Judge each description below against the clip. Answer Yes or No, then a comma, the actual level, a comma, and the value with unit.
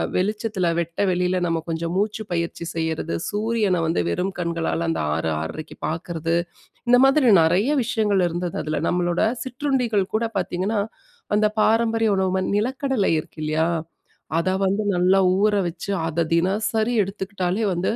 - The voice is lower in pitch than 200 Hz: Yes, medium, 185 Hz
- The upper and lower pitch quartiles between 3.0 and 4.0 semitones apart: No, average, 4.4 semitones